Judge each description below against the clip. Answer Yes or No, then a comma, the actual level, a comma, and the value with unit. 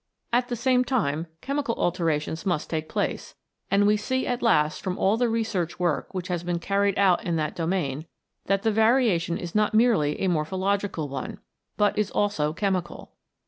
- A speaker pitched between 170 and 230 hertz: Yes, high, 190 Hz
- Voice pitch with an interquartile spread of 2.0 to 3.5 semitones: No, average, 4.7 semitones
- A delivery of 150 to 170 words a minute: No, average, 180 wpm